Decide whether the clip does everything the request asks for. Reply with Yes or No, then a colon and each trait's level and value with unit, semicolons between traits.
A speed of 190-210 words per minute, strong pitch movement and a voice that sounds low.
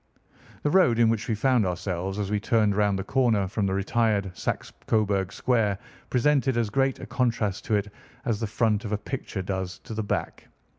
No: average, 200 wpm; average, 3.0 semitones; low, 105 Hz